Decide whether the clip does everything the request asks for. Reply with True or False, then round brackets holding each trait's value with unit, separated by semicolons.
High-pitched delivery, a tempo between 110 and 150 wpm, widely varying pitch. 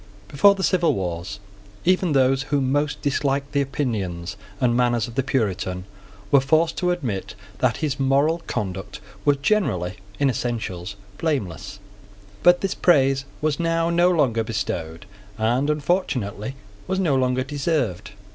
False (135 Hz; 140 wpm; 6.6 semitones)